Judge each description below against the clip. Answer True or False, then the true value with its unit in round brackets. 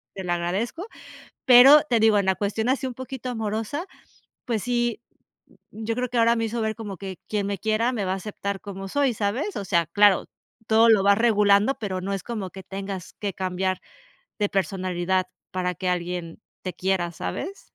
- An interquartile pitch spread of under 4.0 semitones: True (3.6 semitones)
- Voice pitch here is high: True (205 Hz)